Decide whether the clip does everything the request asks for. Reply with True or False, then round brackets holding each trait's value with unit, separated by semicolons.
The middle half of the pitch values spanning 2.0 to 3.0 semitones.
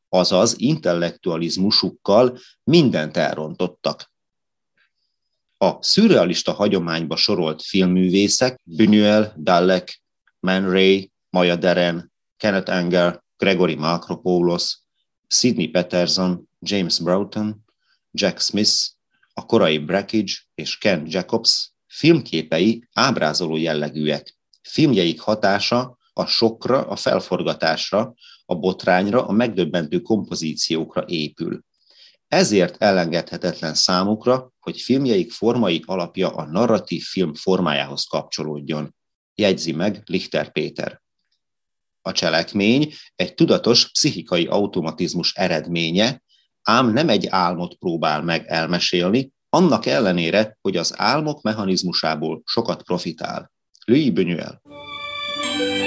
False (3.9 semitones)